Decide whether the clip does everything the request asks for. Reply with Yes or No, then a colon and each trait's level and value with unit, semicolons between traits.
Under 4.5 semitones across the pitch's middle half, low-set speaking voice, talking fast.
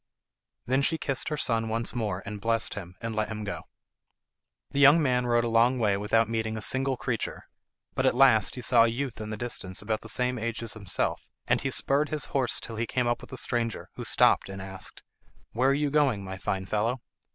Yes: average, 3.1 semitones; low, 115 Hz; fast, 225 wpm